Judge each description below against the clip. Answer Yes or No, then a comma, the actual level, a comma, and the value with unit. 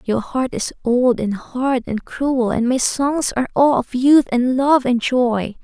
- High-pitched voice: Yes, very high, 250 Hz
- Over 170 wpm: Yes, average, 200 wpm